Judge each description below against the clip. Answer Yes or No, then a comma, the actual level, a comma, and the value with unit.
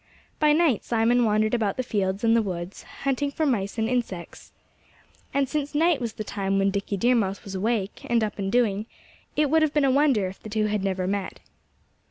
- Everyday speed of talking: No, fast, 215 wpm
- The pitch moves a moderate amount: Yes, average, 4.9 semitones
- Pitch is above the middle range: Yes, high, 220 Hz